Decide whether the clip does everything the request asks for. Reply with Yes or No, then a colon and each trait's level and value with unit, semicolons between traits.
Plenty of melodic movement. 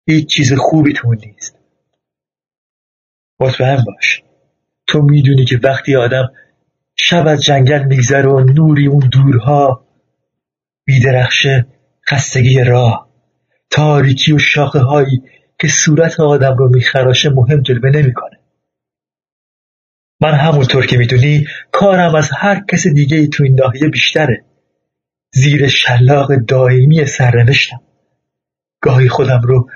No: narrow, 2.4 semitones